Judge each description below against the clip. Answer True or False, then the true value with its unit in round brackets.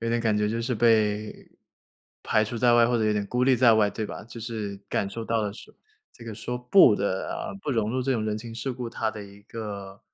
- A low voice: True (110 Hz)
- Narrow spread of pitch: True (2.1 semitones)